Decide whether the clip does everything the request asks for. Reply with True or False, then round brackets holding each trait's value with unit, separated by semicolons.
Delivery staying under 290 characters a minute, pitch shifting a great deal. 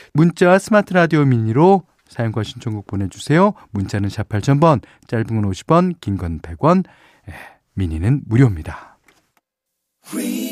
True (245 characters per minute; 8.5 semitones)